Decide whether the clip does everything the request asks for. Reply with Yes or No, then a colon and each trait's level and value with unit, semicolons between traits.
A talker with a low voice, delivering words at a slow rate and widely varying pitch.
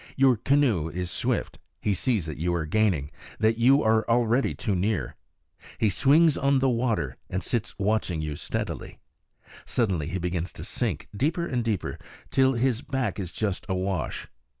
No: low, 110 Hz; average, 165 wpm; wide, 6.1 semitones